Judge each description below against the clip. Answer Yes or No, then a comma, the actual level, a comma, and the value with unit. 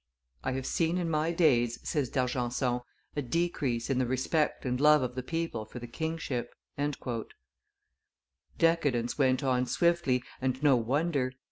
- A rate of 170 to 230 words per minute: No, average, 145 wpm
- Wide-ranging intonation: No, average, 4.2 semitones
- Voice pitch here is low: Yes, low, 130 Hz